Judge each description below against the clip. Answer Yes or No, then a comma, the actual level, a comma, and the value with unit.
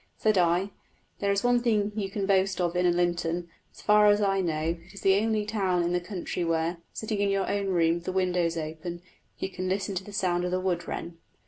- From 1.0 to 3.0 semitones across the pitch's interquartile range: Yes, narrow, 2.5 semitones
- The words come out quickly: Yes, fast, 235 wpm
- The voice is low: No, medium, 185 Hz